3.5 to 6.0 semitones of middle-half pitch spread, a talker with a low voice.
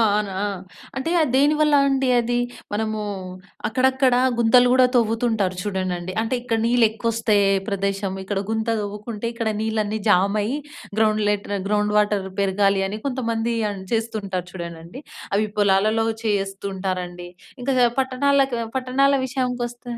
No: average, 3.8 semitones; high, 220 Hz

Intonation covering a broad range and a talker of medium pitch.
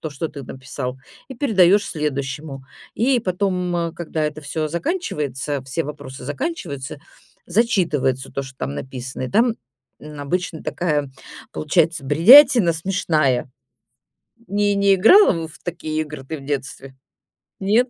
Yes: wide, 5.7 semitones; medium, 155 Hz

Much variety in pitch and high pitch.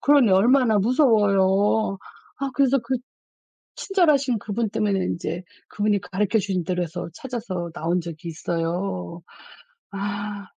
No: average, 4.7 semitones; high, 205 Hz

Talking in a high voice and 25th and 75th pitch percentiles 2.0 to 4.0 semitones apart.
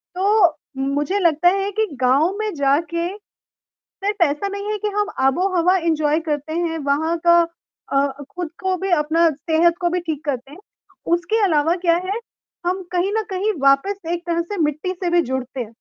No: very high, 340 Hz; average, 4.4 semitones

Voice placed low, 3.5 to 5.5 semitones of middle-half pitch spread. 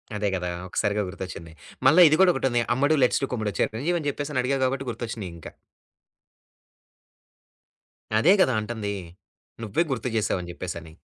Yes: low, 120 Hz; average, 5.2 semitones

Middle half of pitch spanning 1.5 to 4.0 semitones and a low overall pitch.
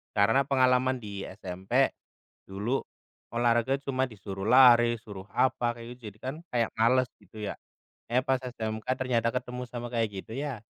Yes: average, 2.9 semitones; low, 120 Hz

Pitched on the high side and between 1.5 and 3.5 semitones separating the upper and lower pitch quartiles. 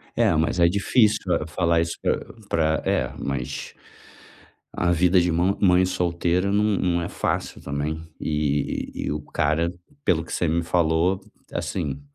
No: very low, 85 Hz; narrow, 2.5 semitones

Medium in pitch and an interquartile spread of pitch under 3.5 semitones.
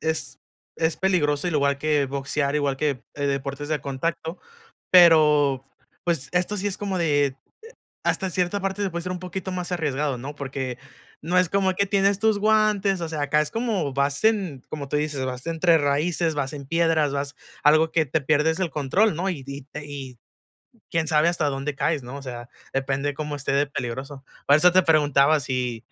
No: medium, 150 Hz; average, 4.0 semitones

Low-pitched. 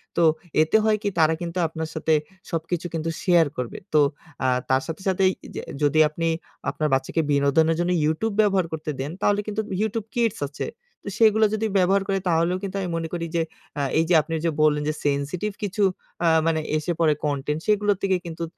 No: medium, 170 Hz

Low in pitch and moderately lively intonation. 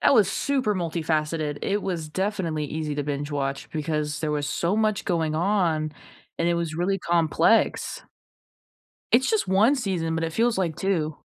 No: medium, 170 Hz; average, 4.2 semitones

